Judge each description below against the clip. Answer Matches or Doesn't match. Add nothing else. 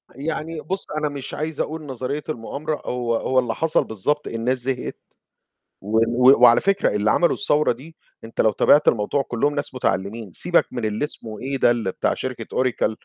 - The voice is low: Matches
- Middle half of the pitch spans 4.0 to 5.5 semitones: Matches